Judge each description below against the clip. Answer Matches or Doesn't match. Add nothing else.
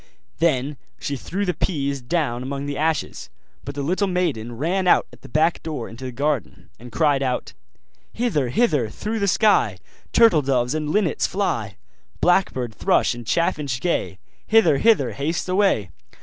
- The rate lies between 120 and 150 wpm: Doesn't match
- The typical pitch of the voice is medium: Matches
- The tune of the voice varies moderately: Doesn't match